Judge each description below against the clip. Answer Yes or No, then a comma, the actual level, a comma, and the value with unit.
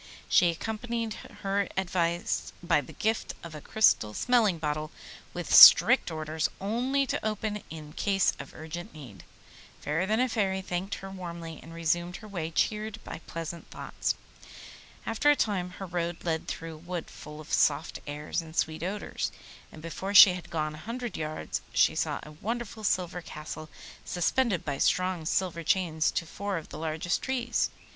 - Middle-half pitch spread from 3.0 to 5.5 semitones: Yes, average, 4.5 semitones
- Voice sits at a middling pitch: Yes, medium, 175 Hz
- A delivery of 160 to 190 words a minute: Yes, average, 170 wpm